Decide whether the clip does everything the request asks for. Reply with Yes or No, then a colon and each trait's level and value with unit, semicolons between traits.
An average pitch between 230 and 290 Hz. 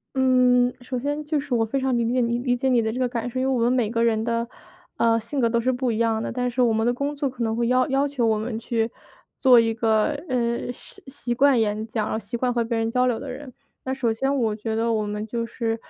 Yes: high, 240 Hz